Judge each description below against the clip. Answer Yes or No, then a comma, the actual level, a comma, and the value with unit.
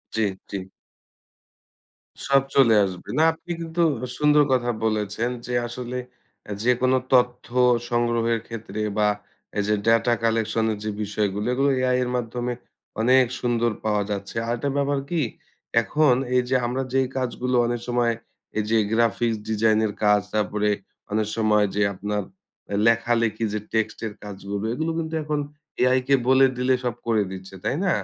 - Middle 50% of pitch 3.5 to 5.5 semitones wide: No, average, 3.1 semitones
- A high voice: No, low, 115 Hz